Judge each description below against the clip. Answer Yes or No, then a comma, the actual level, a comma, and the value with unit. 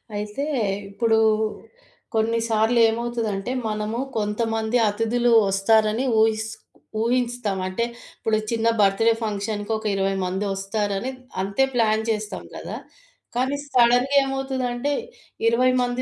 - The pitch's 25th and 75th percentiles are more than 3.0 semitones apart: No, narrow, 2.5 semitones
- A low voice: No, high, 225 Hz